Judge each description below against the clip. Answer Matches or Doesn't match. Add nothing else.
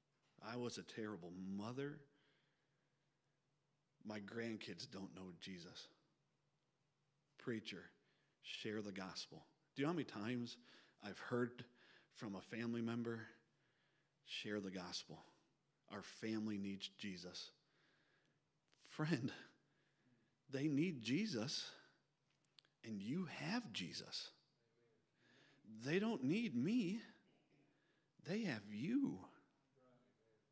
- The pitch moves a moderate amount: Doesn't match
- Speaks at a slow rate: Matches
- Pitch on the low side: Matches